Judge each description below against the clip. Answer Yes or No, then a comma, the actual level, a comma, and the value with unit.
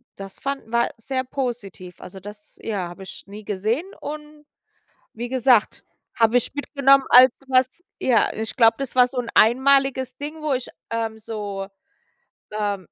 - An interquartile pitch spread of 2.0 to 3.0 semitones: No, average, 4.2 semitones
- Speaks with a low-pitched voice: No, high, 240 Hz